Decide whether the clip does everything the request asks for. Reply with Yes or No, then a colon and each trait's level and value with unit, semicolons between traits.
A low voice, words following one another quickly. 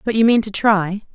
No: high, 210 Hz; fast, 260 wpm